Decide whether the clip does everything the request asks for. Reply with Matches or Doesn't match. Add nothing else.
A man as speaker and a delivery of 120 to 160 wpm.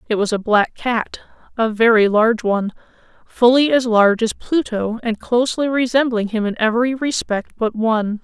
Doesn't match